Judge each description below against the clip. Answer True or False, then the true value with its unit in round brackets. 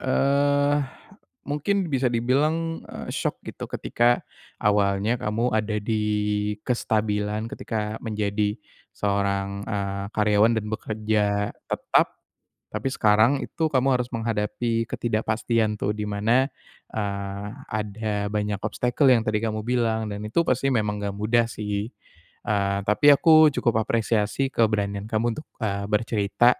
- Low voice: True (110 Hz)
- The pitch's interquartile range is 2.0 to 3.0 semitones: True (2.6 semitones)